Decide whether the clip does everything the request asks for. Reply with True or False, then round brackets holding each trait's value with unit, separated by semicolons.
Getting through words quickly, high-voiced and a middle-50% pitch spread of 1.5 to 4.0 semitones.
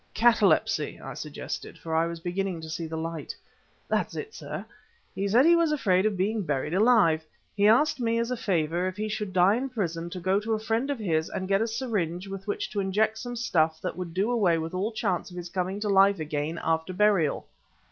False (220 wpm; 195 Hz; 4.7 semitones)